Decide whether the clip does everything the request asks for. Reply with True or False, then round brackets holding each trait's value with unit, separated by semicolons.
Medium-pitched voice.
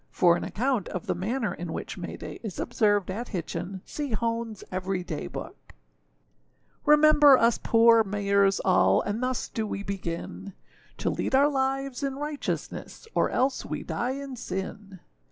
False (220 Hz)